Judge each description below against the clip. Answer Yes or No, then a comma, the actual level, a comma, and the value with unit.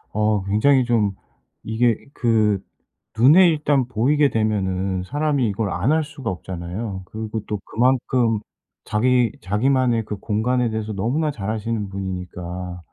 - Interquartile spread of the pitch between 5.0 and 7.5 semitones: No, average, 4.2 semitones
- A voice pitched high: No, low, 110 Hz